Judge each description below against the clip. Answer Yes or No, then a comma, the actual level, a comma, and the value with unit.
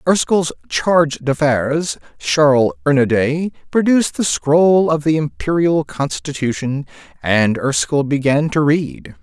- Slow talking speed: Yes, slow, 110 wpm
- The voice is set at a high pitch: No, medium, 145 Hz